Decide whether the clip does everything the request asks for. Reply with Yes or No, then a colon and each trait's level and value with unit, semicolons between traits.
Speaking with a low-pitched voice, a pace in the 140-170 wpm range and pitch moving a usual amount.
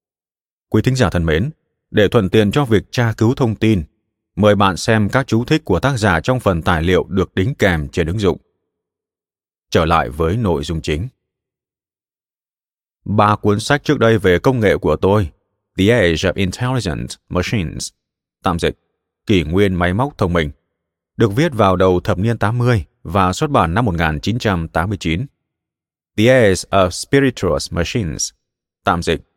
Yes: low, 100 Hz; slow, 165 wpm; average, 4.9 semitones